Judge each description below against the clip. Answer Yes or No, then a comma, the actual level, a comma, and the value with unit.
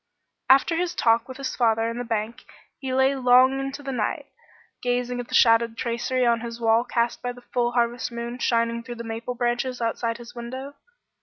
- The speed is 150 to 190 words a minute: No, average, 200 wpm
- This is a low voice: No, high, 240 Hz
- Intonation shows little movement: Yes, narrow, 1.6 semitones